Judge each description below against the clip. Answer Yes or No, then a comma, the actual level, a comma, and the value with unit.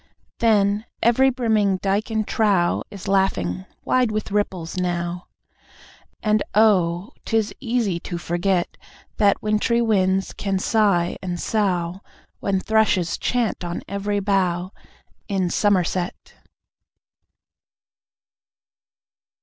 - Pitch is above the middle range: Yes, high, 195 Hz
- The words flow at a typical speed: No, slow, 100 wpm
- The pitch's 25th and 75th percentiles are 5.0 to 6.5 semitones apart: No, average, 3.3 semitones